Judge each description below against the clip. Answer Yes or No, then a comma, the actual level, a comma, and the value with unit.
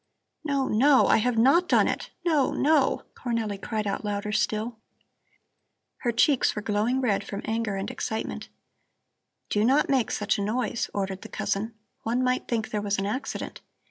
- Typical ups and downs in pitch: Yes, average, 3.6 semitones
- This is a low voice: No, high, 225 Hz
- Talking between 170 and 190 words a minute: Yes, average, 175 wpm